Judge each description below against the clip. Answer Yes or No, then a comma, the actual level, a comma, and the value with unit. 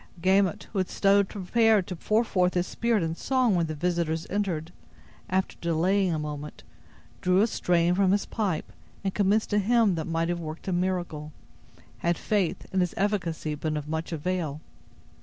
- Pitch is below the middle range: No, medium, 180 Hz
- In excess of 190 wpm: No, average, 175 wpm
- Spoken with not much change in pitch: No, average, 3.5 semitones